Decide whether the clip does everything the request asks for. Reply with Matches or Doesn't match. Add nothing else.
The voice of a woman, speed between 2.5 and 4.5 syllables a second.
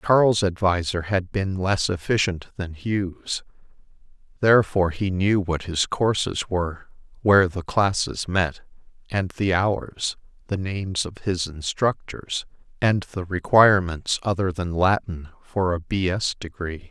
Doesn't match